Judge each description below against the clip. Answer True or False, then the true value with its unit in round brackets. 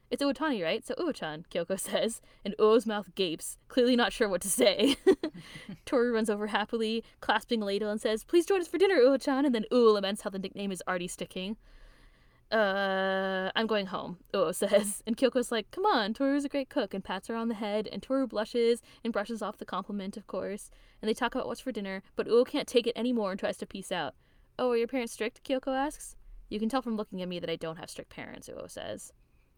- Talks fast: True (230 wpm)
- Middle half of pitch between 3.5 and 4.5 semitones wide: True (3.9 semitones)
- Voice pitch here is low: False (220 Hz)